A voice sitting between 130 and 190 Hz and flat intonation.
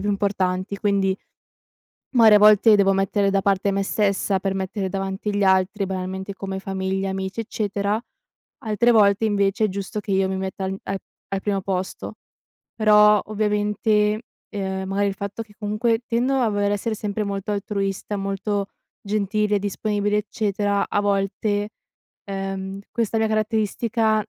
No: high, 200 Hz; narrow, 1.5 semitones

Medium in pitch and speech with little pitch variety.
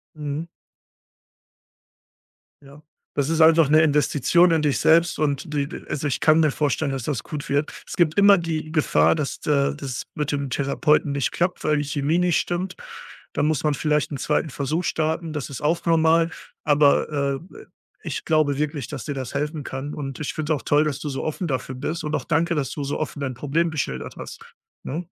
Yes: medium, 150 Hz; narrow, 2.2 semitones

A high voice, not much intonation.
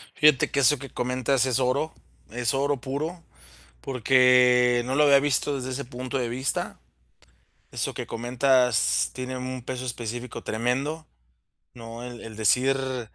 No: low, 125 Hz; narrow, 1.9 semitones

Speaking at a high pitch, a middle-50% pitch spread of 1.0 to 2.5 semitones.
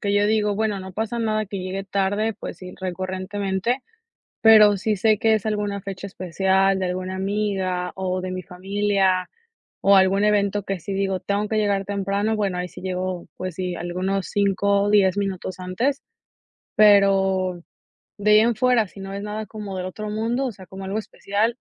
Yes: high, 195 Hz; narrow, 2.0 semitones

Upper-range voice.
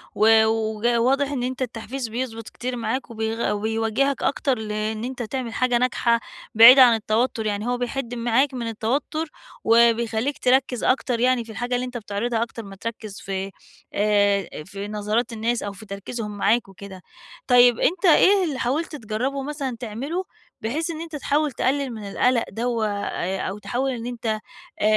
Yes: high, 235 Hz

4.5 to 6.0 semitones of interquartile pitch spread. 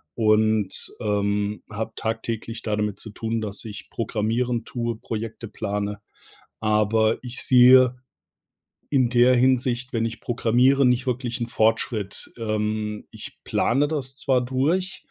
No: average, 2.7 semitones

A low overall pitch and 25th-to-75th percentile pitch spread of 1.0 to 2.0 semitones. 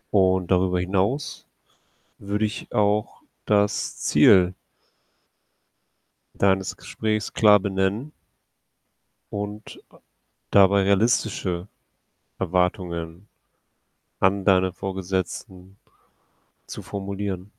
Yes: very low, 95 Hz; narrow, 1.7 semitones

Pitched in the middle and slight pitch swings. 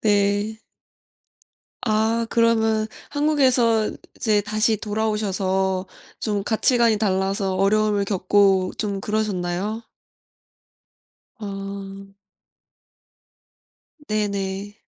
No: high, 205 Hz; narrow, 1.9 semitones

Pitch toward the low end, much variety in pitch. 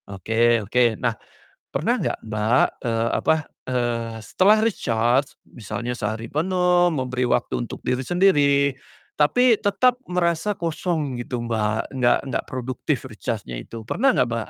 Yes: low, 125 Hz; wide, 6.7 semitones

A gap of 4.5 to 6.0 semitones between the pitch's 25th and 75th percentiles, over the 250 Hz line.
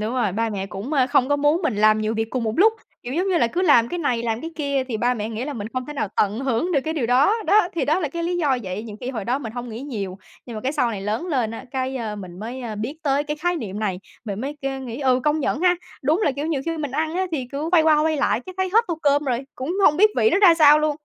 Yes: wide, 5.5 semitones; very high, 265 Hz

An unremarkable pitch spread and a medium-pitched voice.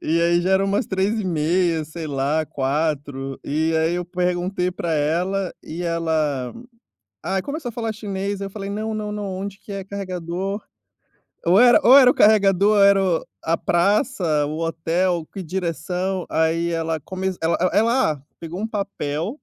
Yes: average, 3.5 semitones; medium, 180 Hz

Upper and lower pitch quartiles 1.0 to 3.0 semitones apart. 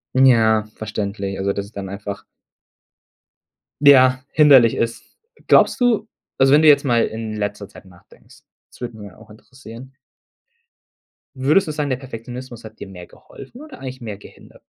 No: average, 4.2 semitones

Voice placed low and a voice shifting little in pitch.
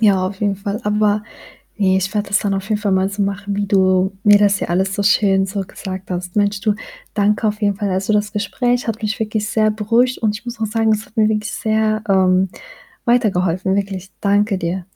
No: high, 205 Hz; narrow, 2.0 semitones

